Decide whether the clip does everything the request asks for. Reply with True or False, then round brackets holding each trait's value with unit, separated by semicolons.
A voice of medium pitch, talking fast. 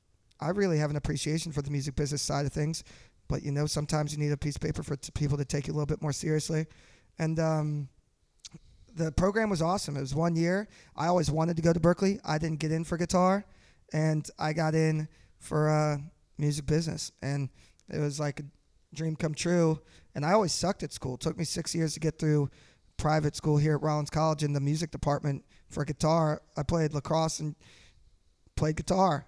True (155 Hz; 215 wpm)